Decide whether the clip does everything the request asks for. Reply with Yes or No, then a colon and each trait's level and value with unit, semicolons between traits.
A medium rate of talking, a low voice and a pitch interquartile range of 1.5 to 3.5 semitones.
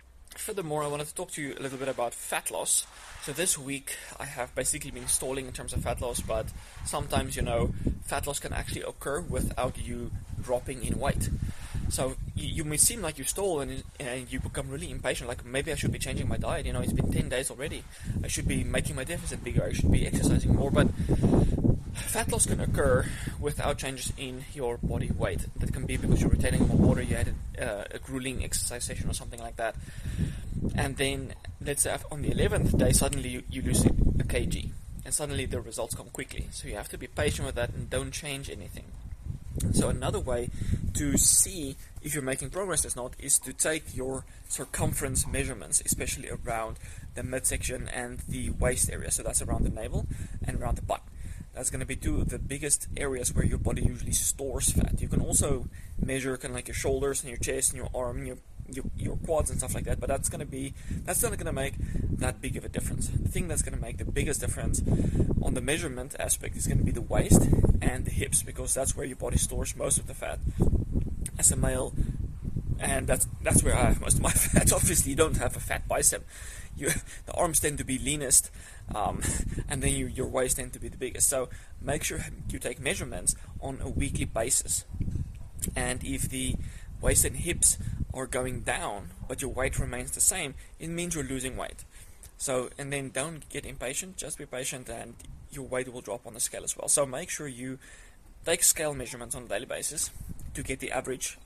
No: fast, 215 wpm; low, 130 Hz; average, 3.2 semitones